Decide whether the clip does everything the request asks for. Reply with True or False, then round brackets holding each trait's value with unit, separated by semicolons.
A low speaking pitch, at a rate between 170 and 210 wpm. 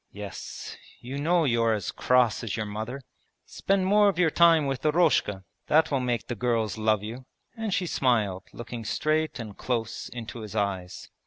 True (120 Hz; 175 wpm)